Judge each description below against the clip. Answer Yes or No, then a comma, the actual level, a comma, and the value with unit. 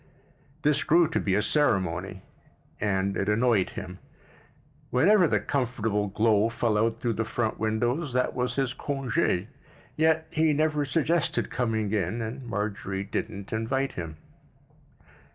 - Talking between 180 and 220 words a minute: No, slow, 135 wpm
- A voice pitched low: Yes, low, 115 Hz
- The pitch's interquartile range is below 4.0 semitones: No, average, 5.0 semitones